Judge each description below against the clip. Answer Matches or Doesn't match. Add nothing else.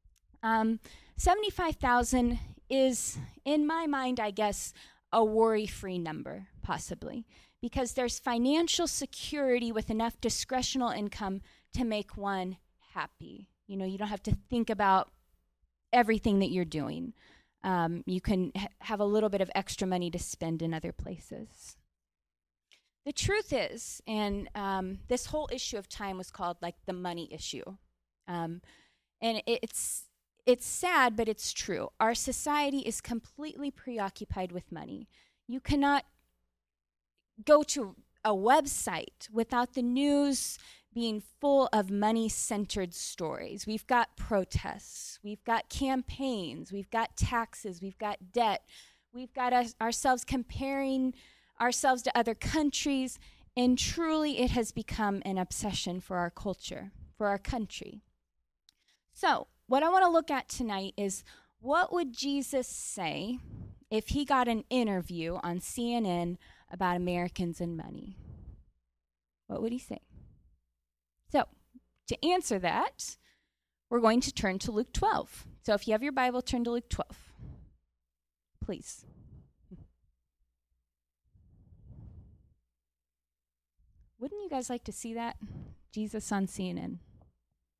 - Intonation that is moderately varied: Doesn't match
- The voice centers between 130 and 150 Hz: Doesn't match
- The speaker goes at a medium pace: Doesn't match